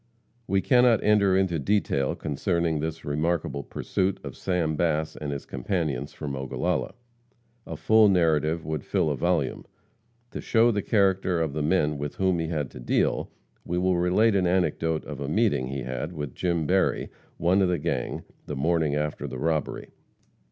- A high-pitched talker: No, very low, 80 Hz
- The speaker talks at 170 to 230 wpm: Yes, average, 175 wpm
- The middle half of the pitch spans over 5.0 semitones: No, average, 4.1 semitones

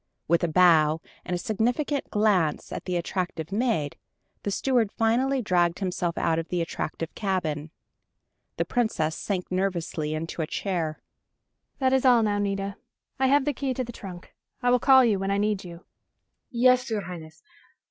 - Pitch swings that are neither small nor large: No, wide, 5.8 semitones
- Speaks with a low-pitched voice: No, high, 195 Hz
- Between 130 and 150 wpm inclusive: No, average, 170 wpm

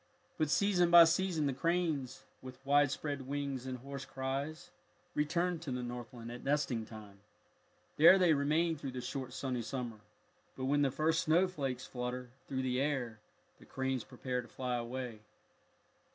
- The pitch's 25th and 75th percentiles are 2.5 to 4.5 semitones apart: Yes, average, 3.5 semitones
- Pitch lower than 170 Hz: Yes, low, 135 Hz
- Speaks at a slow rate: No, average, 160 wpm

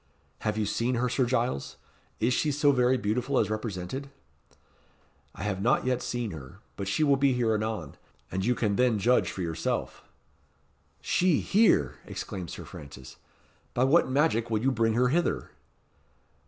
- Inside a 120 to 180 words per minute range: Yes, average, 165 wpm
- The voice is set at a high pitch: No, low, 120 Hz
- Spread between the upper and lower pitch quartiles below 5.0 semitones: Yes, average, 4.2 semitones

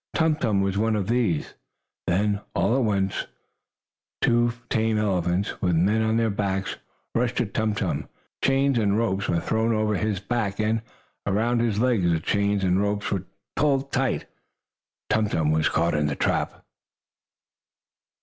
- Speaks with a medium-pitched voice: No, low, 105 Hz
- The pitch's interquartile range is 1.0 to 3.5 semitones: Yes, average, 3.1 semitones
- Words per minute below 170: Yes, average, 160 wpm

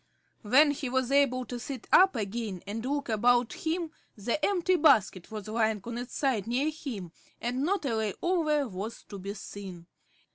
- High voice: Yes, high, 245 Hz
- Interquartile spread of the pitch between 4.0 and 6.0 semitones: Yes, average, 5.2 semitones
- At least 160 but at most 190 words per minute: Yes, average, 180 wpm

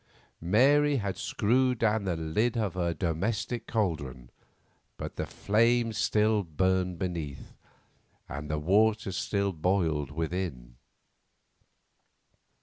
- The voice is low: Yes, very low, 95 Hz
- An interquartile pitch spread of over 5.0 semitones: Yes, wide, 5.4 semitones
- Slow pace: Yes, slow, 105 wpm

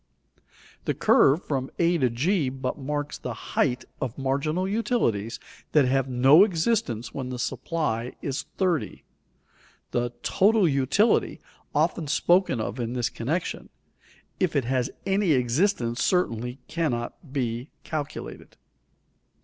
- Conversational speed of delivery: No, slow, 120 wpm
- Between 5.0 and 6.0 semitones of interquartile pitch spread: Yes, wide, 5.6 semitones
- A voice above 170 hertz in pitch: No, medium, 140 Hz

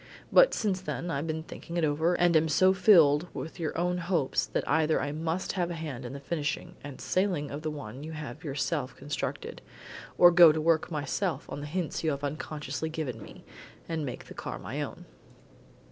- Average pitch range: Yes, average, 3.0 semitones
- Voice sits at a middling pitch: Yes, medium, 155 Hz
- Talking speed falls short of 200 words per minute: No, fast, 205 wpm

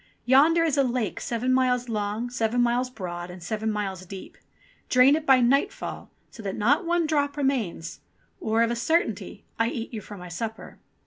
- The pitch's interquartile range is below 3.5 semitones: No, average, 4.2 semitones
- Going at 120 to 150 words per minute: No, average, 180 wpm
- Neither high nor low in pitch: No, high, 240 Hz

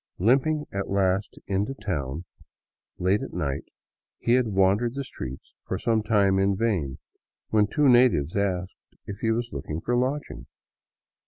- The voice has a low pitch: Yes, low, 100 Hz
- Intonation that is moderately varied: Yes, average, 4.5 semitones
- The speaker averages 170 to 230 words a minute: No, average, 150 wpm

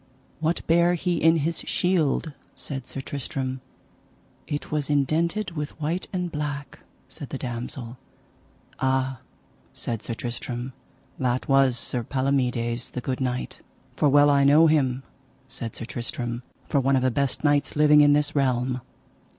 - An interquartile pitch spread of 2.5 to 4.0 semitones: Yes, average, 3.1 semitones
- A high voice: No, medium, 140 Hz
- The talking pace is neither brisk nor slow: Yes, average, 150 wpm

